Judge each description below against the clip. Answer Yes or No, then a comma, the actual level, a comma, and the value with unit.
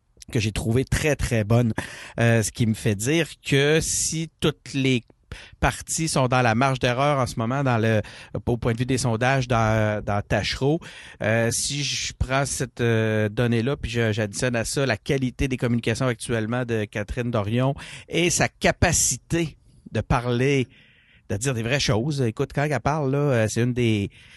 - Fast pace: No, average, 180 wpm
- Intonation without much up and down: No, average, 3.5 semitones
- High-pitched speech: No, low, 125 Hz